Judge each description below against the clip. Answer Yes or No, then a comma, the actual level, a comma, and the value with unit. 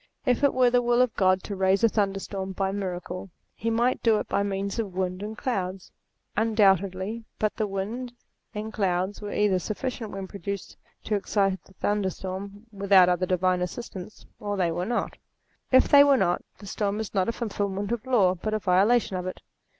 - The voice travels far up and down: No, average, 2.8 semitones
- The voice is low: No, high, 200 Hz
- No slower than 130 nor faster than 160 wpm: No, average, 190 wpm